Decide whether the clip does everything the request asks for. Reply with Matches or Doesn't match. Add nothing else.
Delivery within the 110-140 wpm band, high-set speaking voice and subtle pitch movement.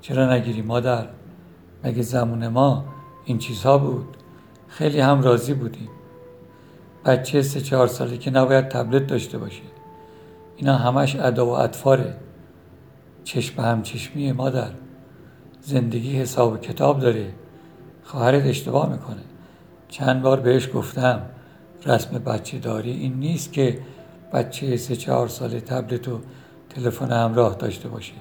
Doesn't match